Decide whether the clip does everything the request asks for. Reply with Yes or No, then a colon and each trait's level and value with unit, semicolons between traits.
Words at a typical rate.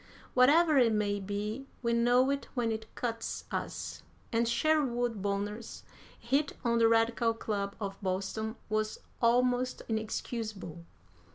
No: slow, 125 wpm